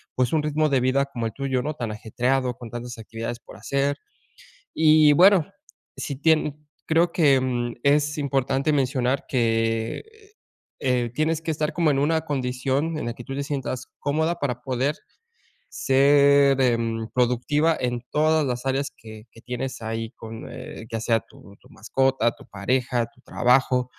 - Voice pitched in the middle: No, low, 130 Hz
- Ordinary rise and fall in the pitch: Yes, average, 3.3 semitones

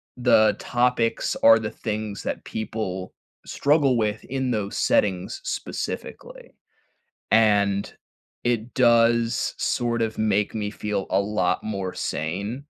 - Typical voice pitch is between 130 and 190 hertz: No, low, 110 Hz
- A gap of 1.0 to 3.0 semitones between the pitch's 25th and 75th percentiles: Yes, narrow, 2.6 semitones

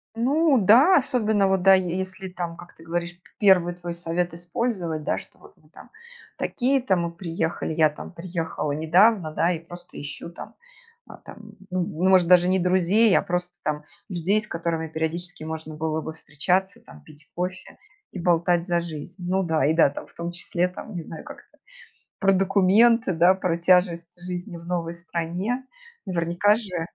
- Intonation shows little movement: Yes, narrow, 2.3 semitones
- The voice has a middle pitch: Yes, medium, 175 Hz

